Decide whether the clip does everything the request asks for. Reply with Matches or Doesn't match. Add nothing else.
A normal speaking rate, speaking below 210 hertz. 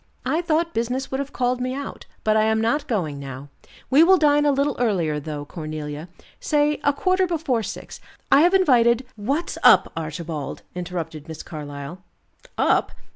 Doesn't match